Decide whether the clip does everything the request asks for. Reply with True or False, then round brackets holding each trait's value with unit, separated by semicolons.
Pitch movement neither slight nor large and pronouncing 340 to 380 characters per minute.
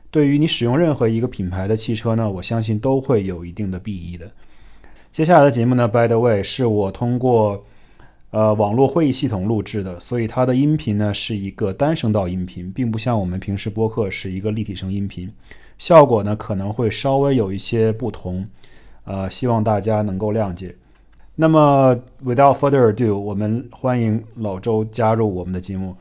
False (3.7 semitones; 330 characters per minute)